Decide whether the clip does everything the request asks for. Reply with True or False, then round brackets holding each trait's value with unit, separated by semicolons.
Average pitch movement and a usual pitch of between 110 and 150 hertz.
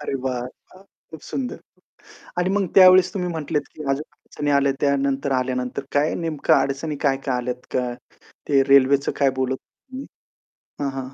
True (3.3 semitones; 140 Hz)